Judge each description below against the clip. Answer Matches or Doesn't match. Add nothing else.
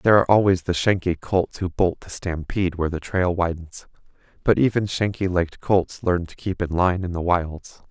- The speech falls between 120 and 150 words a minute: Doesn't match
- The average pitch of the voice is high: Doesn't match